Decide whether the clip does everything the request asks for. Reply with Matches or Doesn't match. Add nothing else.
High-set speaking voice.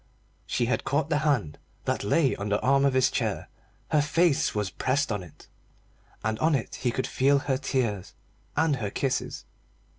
Doesn't match